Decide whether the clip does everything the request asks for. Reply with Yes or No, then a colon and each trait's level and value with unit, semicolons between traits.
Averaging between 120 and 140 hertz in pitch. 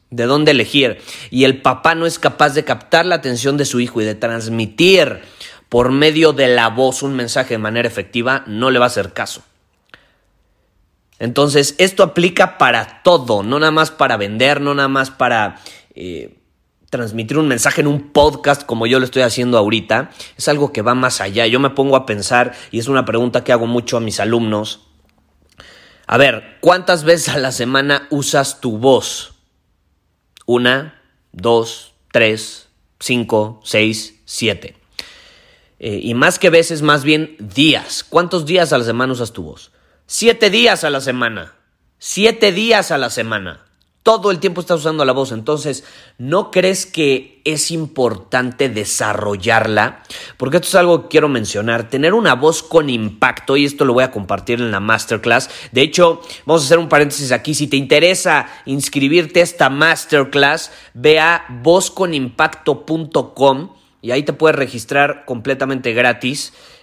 Yes: low, 135 Hz